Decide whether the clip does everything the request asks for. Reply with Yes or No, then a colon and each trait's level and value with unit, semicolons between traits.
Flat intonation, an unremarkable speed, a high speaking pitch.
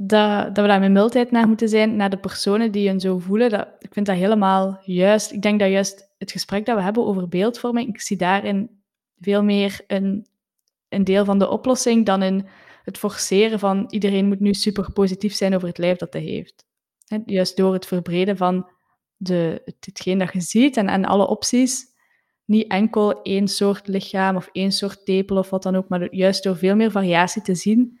No: narrow, 1.7 semitones; fast, 205 wpm; high, 200 Hz